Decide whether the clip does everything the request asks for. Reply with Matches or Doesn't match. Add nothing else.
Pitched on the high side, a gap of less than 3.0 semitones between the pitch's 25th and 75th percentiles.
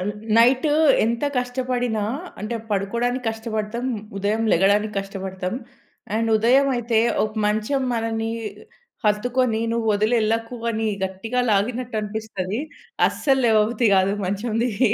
Matches